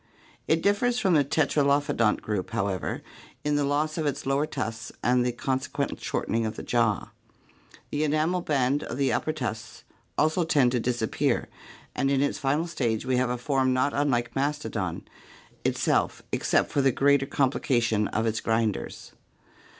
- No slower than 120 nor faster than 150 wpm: No, average, 160 wpm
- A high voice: No, low, 135 Hz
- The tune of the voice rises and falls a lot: No, average, 3.7 semitones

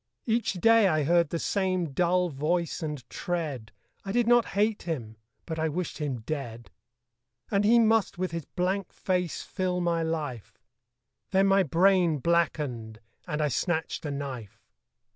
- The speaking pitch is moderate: Yes, medium, 170 Hz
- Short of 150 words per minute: No, average, 155 wpm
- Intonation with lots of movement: No, average, 4.3 semitones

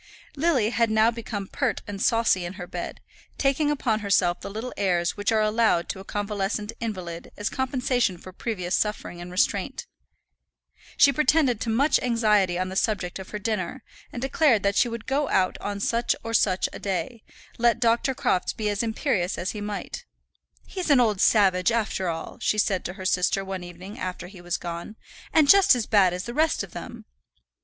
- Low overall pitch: No, high, 210 Hz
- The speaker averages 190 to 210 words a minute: Yes, average, 195 wpm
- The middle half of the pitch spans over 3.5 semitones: Yes, average, 4.1 semitones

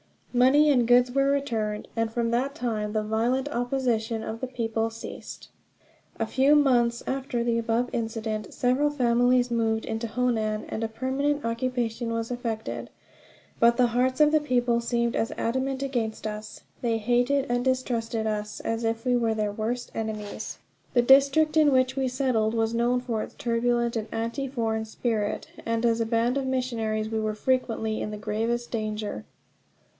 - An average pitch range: No, narrow, 2.3 semitones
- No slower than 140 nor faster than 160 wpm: No, average, 170 wpm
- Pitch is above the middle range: Yes, high, 235 Hz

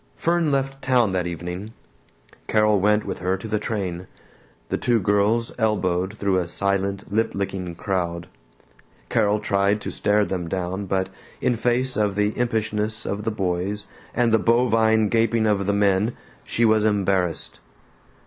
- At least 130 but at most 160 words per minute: Yes, average, 155 wpm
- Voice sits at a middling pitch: No, low, 105 Hz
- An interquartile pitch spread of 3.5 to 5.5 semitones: No, average, 2.7 semitones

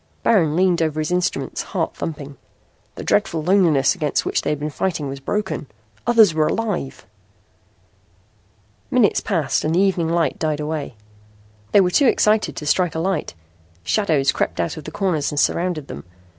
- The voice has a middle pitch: Yes, medium, 160 Hz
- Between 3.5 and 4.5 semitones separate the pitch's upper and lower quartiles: Yes, average, 3.8 semitones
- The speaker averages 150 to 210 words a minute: Yes, average, 170 wpm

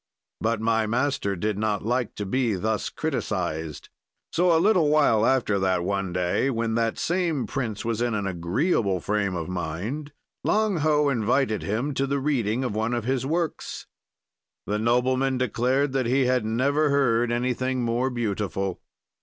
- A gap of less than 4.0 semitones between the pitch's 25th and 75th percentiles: No, average, 4.4 semitones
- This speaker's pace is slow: No, average, 160 wpm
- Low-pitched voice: Yes, low, 120 Hz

